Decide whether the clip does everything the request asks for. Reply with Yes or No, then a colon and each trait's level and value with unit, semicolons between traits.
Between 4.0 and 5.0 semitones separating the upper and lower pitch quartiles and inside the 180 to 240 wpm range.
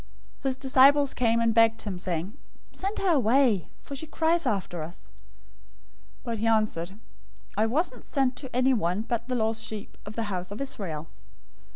No: average, 4.6 semitones; average, 170 wpm